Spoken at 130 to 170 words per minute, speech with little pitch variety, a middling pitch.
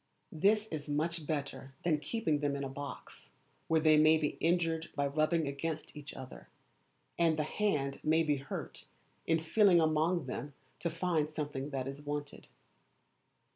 Yes: average, 165 wpm; narrow, 2.3 semitones; medium, 155 Hz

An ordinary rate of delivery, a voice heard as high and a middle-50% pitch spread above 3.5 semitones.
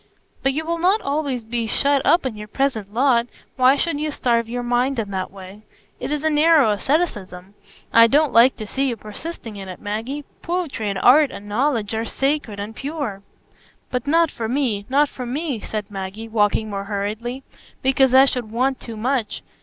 Yes: average, 190 wpm; high, 245 Hz; average, 4.9 semitones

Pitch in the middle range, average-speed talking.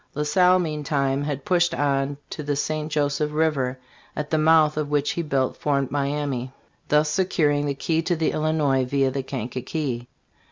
Yes: medium, 145 Hz; average, 170 wpm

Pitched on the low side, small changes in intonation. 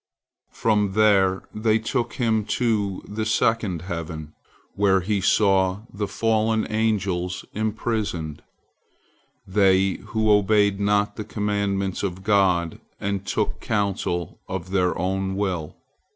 Yes: low, 100 Hz; narrow, 2.3 semitones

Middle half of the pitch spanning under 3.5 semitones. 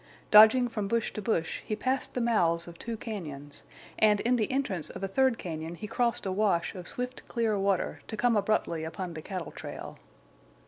No: average, 5.2 semitones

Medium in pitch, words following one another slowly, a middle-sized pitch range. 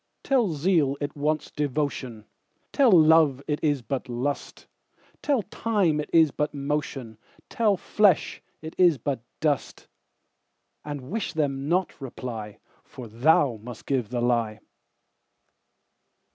Yes: medium, 145 Hz; slow, 105 wpm; average, 4.2 semitones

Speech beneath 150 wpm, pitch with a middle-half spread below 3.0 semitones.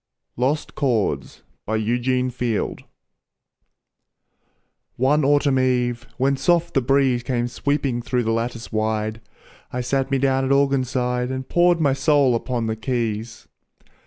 Yes: slow, 135 wpm; narrow, 2.5 semitones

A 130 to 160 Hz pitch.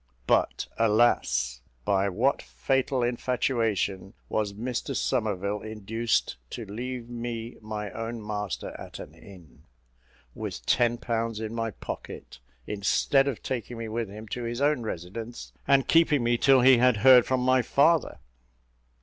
No: low, 115 Hz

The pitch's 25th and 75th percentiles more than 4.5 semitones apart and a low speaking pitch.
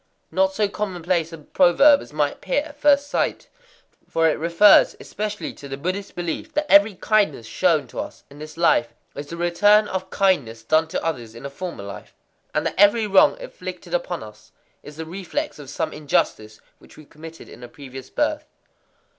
No: wide, 5.5 semitones; medium, 170 Hz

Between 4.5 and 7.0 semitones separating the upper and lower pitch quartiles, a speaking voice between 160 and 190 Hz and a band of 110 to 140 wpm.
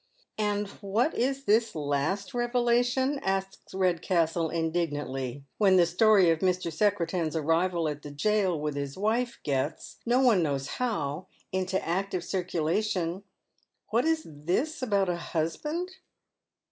Yes: average, 5.0 semitones; medium, 185 Hz; slow, 135 wpm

